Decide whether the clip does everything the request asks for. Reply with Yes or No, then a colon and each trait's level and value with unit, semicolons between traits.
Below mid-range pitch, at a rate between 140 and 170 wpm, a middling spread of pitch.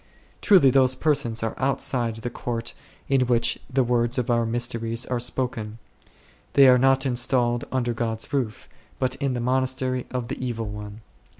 No: low, 120 Hz; average, 165 wpm; narrow, 2.0 semitones